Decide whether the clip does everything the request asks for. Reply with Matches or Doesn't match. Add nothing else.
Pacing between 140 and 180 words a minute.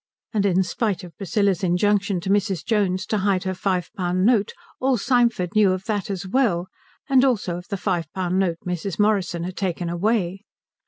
Doesn't match